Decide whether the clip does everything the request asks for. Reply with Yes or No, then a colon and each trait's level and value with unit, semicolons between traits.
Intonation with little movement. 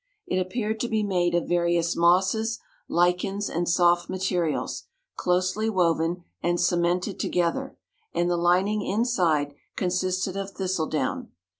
Yes: narrow, 2.2 semitones